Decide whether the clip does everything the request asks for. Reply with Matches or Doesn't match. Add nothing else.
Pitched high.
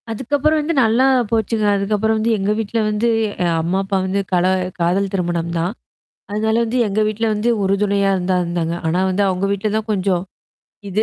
Matches